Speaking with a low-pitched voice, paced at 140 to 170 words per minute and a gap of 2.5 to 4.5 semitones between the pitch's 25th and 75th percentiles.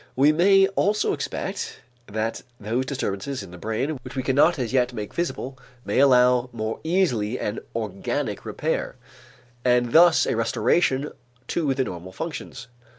No: low, 125 Hz; average, 150 wpm; average, 5.0 semitones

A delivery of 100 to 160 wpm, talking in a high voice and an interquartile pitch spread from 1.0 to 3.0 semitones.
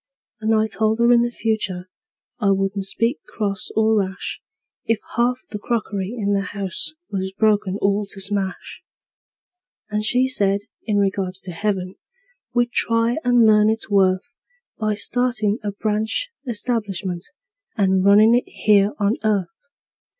Yes: average, 145 wpm; high, 210 Hz; narrow, 2.6 semitones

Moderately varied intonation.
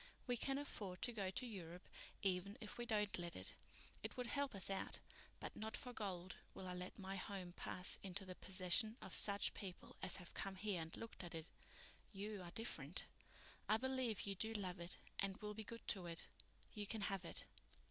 Yes: average, 3.3 semitones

